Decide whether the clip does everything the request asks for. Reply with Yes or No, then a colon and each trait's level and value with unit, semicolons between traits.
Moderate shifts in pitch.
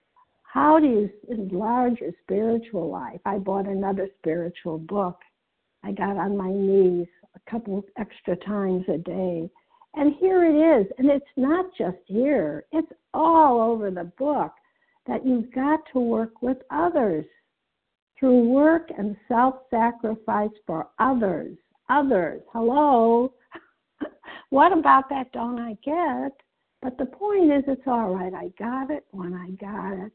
No: wide, 6.5 semitones